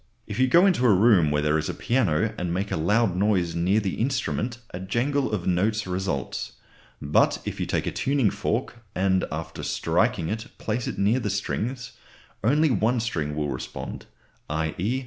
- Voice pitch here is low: Yes, low, 100 Hz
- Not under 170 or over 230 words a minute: Yes, average, 185 wpm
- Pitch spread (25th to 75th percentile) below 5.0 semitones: No, wide, 5.6 semitones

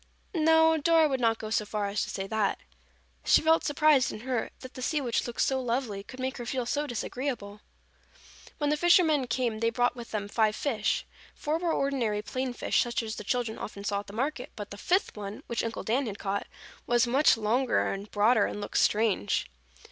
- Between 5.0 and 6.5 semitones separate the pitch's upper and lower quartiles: No, average, 4.4 semitones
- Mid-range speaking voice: No, high, 240 Hz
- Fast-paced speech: Yes, fast, 210 wpm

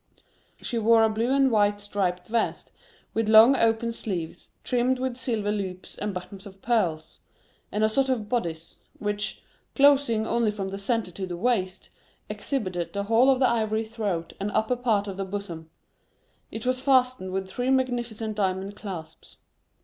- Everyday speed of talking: Yes, average, 165 wpm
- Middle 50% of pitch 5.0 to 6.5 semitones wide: No, average, 3.7 semitones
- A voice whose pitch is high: Yes, high, 215 Hz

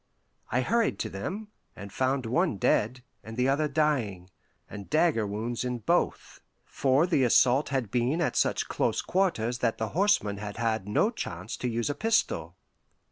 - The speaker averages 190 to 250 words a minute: No, average, 170 wpm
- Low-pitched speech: Yes, low, 125 Hz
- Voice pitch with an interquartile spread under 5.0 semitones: No, wide, 5.6 semitones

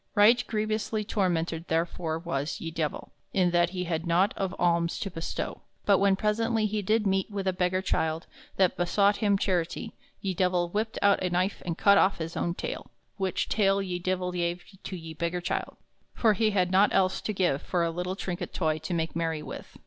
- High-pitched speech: No, medium, 180 Hz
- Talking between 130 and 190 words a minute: No, average, 200 wpm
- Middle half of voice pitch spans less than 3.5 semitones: Yes, average, 2.8 semitones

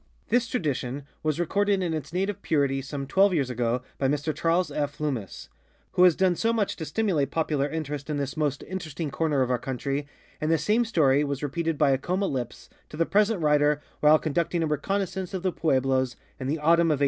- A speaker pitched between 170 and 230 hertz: No, medium, 155 Hz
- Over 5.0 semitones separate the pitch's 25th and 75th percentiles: No, average, 4.2 semitones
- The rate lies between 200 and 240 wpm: Yes, fast, 205 wpm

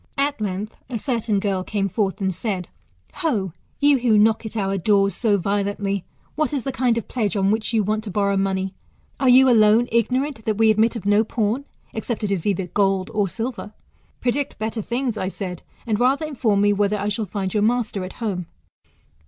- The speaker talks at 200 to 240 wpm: Yes, fast, 205 wpm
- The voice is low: No, high, 215 Hz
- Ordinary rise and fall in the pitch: Yes, average, 3.0 semitones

